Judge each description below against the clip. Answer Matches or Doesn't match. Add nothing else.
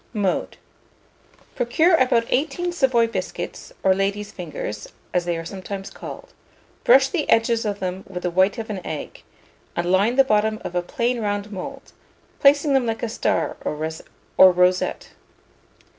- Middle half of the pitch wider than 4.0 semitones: Matches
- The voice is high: Matches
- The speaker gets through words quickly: Doesn't match